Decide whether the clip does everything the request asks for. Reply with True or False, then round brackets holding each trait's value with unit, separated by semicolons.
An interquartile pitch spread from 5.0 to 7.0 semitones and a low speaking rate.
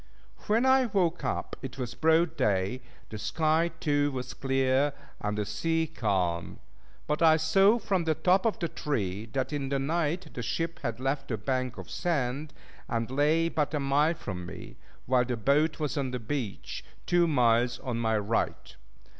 False (5.6 semitones; 180 wpm)